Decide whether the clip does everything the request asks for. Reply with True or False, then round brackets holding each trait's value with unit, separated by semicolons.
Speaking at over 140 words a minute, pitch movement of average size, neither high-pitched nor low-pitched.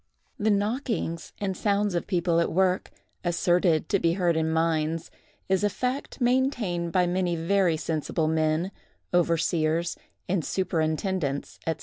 False (135 wpm; 3.1 semitones; 175 Hz)